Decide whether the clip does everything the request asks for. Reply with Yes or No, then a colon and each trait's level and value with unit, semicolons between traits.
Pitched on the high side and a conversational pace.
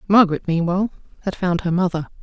No: medium, 180 Hz; average, 160 wpm